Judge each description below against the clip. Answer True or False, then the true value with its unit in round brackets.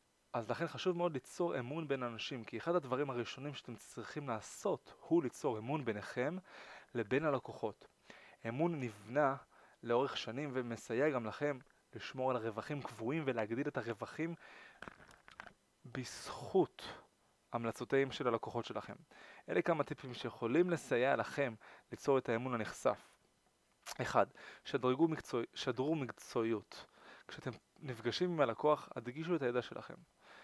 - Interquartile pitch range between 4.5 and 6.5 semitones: False (4.1 semitones)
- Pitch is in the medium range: False (130 Hz)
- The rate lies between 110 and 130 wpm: True (125 wpm)